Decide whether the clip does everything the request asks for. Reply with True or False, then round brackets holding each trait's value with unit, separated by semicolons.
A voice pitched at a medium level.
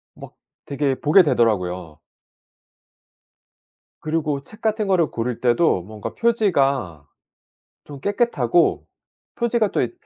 True (145 Hz)